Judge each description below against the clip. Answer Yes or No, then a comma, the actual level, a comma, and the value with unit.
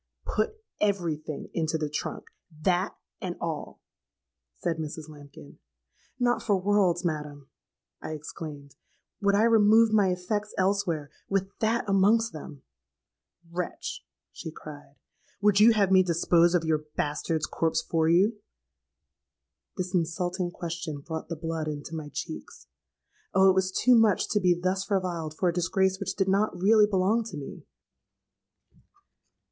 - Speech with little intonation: No, average, 4.3 semitones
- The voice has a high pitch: No, medium, 180 Hz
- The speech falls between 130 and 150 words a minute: Yes, slow, 135 wpm